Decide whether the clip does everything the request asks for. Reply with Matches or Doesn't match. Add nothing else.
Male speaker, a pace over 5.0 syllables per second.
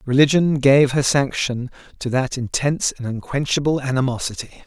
Matches